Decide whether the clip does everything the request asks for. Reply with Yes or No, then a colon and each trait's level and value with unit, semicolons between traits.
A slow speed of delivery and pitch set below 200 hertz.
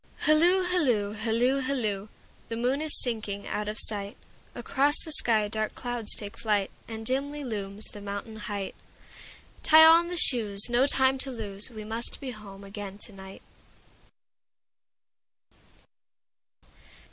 No: slow, 120 wpm; high, 225 Hz